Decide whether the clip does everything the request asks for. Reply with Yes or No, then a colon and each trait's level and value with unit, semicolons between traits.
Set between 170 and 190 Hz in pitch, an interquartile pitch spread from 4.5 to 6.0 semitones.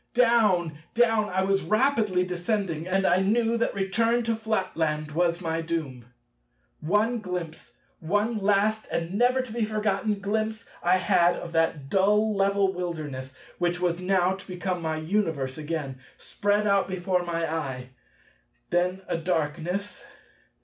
No: medium, 185 Hz; average, 4.1 semitones